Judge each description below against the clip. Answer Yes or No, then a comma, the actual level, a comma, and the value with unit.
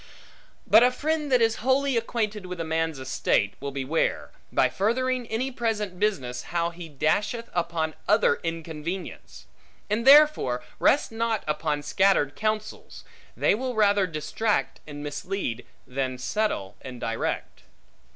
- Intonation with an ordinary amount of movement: No, wide, 7.2 semitones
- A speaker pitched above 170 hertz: Yes, high, 190 Hz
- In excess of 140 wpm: No, slow, 135 wpm